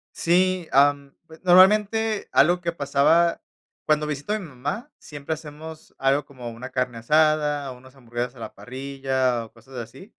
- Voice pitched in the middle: Yes, medium, 145 Hz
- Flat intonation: No, average, 4.6 semitones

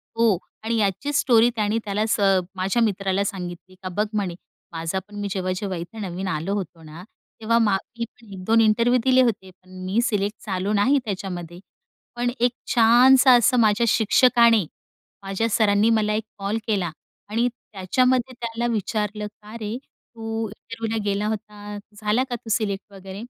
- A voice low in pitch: No, high, 210 Hz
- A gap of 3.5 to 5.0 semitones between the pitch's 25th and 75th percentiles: No, average, 2.9 semitones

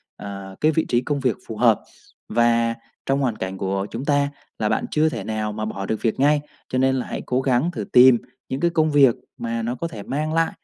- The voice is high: No, low, 125 Hz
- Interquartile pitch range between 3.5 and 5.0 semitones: Yes, average, 4.6 semitones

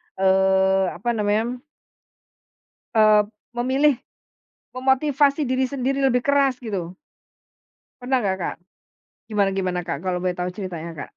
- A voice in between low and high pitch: No, high, 215 Hz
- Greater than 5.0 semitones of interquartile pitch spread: Yes, wide, 5.5 semitones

